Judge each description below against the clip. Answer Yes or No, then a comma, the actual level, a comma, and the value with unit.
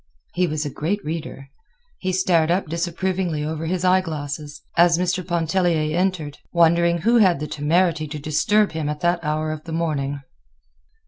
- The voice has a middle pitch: Yes, medium, 165 Hz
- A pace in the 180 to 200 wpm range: No, average, 170 wpm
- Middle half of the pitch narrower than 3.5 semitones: Yes, average, 2.8 semitones